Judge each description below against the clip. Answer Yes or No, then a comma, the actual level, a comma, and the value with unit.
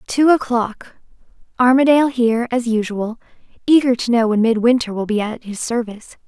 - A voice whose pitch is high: Yes, high, 235 Hz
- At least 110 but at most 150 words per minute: Yes, average, 145 wpm